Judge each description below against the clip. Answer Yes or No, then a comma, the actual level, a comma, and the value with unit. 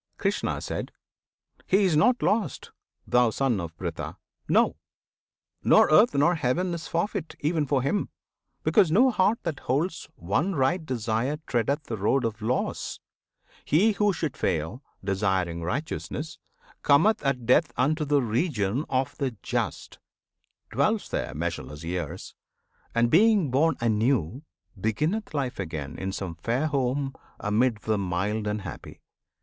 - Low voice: Yes, low, 130 Hz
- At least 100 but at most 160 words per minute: Yes, slow, 135 wpm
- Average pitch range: No, wide, 7.2 semitones